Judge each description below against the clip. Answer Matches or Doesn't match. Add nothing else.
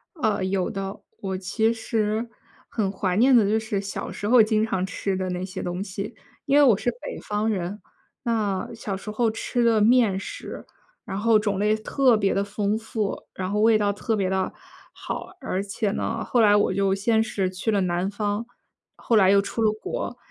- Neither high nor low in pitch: Doesn't match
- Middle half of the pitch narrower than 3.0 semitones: Matches